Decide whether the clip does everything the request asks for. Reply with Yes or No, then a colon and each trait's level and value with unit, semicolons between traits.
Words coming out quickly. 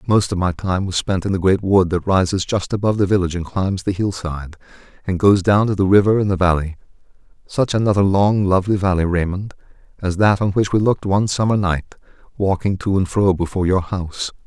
Yes: fast, 210 wpm